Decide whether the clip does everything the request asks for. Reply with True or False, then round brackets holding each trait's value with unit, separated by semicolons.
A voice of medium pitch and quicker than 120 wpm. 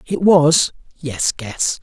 False (150 Hz; 100 wpm)